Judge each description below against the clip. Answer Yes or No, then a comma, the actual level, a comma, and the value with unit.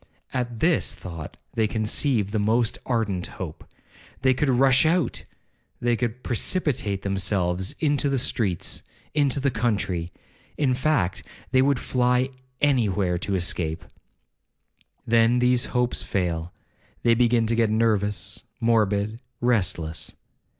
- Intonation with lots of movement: No, average, 4.4 semitones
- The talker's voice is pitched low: Yes, low, 115 Hz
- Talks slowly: Yes, slow, 115 wpm